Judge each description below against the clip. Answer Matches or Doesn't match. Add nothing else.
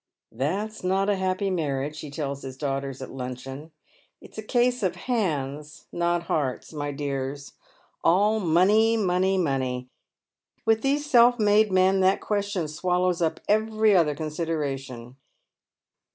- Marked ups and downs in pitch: Matches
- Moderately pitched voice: Matches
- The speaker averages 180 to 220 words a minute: Doesn't match